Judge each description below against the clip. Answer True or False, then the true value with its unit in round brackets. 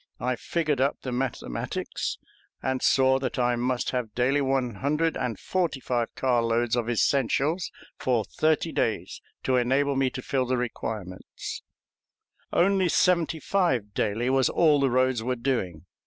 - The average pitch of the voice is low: True (130 Hz)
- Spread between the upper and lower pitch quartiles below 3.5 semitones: True (2.8 semitones)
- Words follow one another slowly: False (155 wpm)